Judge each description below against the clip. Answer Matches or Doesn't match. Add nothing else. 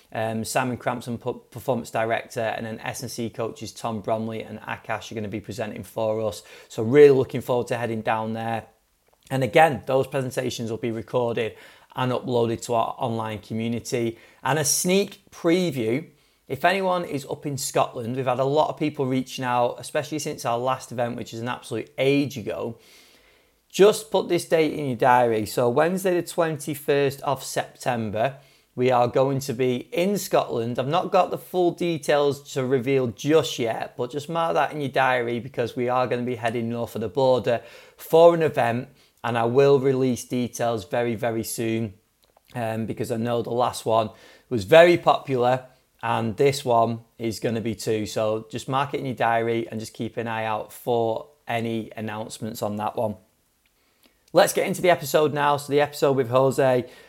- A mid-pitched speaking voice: Doesn't match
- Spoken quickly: Doesn't match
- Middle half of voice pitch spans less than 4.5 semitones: Matches